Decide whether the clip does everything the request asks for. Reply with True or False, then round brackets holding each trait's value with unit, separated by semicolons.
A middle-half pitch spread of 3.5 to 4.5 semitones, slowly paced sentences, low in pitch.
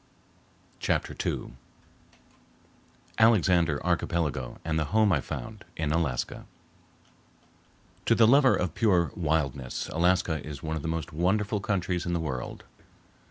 True (4.0 semitones; 125 wpm; 85 Hz)